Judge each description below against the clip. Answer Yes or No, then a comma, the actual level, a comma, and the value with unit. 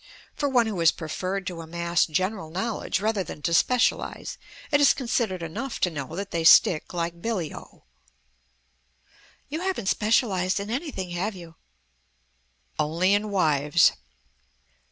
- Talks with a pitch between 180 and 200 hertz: Yes, medium, 185 Hz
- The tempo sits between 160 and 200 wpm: No, average, 140 wpm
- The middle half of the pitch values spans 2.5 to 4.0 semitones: No, average, 4.8 semitones